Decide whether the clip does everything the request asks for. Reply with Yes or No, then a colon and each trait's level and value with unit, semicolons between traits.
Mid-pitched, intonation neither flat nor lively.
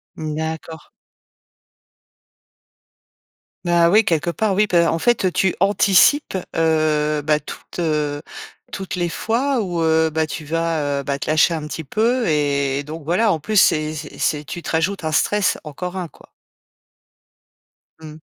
Yes: medium, 160 Hz; average, 3.5 semitones